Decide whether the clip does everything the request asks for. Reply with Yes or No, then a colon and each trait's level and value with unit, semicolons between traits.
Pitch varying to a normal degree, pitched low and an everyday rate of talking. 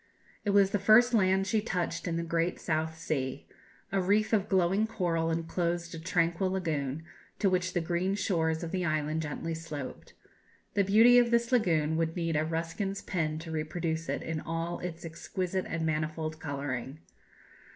No: average, 3.0 semitones; medium, 170 Hz; average, 170 wpm